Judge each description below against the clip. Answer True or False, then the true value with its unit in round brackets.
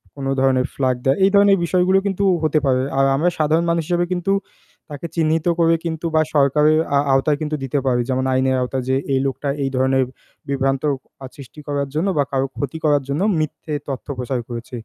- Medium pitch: True (145 Hz)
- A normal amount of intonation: True (3.4 semitones)